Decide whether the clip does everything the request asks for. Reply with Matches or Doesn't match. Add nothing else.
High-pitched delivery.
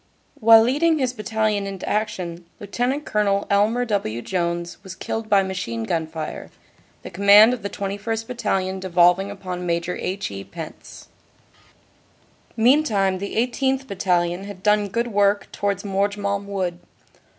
Matches